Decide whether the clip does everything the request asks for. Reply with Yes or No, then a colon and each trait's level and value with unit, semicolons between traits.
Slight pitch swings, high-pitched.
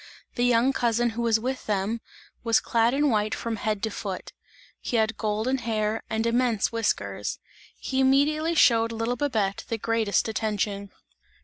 Yes: narrow, 2.2 semitones; high, 230 Hz